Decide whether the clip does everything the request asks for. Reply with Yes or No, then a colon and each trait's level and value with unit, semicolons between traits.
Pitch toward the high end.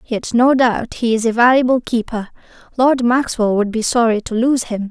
Yes: high, 235 Hz